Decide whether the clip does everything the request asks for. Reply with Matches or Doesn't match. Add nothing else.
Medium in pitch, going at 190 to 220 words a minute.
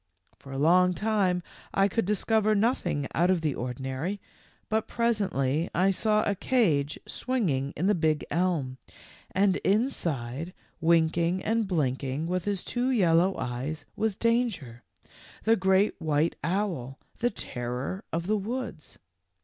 Doesn't match